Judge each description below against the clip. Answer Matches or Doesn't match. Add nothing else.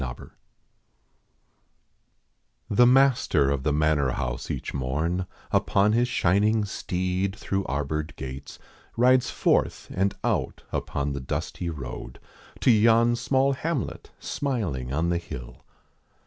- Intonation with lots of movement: Matches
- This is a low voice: Matches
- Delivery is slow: Matches